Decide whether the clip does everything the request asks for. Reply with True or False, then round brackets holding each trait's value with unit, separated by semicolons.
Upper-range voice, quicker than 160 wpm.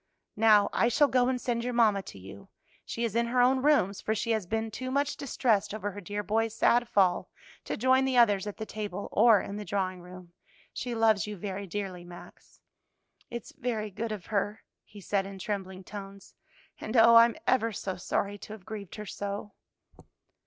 True (210 Hz; 200 wpm)